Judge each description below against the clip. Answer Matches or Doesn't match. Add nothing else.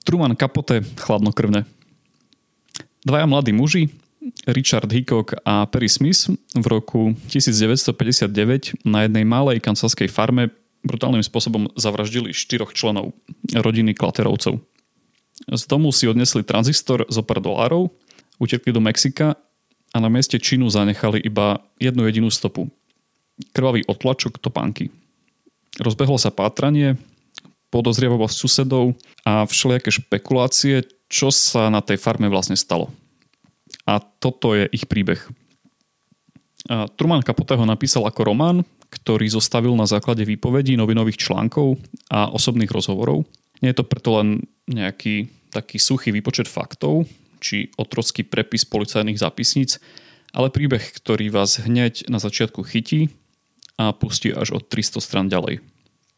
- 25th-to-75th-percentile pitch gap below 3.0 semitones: Doesn't match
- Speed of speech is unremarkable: Matches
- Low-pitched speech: Matches